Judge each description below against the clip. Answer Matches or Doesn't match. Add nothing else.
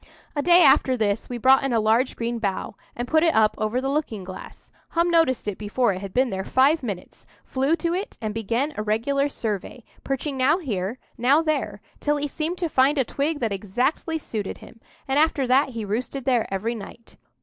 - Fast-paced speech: Matches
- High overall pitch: Matches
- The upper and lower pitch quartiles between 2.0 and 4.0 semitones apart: Doesn't match